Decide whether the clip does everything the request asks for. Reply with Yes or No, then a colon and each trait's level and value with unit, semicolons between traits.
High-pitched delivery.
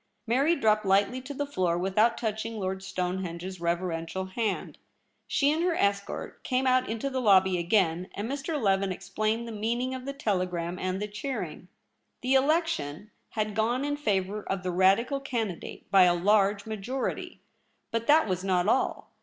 Yes: high, 210 Hz